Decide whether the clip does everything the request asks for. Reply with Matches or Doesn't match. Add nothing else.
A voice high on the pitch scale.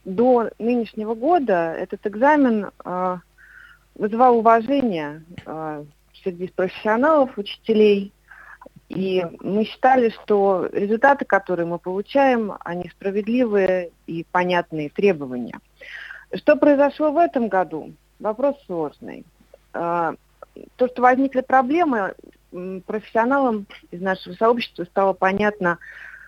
Matches